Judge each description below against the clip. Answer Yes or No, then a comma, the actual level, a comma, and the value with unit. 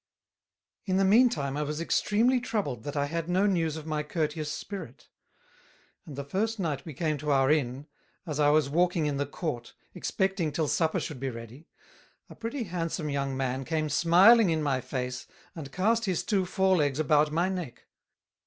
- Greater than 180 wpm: Yes, average, 190 wpm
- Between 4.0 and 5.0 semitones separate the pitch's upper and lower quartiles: Yes, average, 4.7 semitones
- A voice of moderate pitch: Yes, medium, 155 Hz